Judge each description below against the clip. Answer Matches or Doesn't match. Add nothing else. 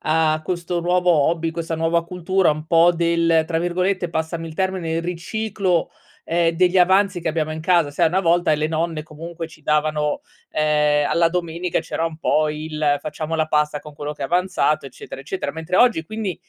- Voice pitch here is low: Doesn't match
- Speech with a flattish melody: Matches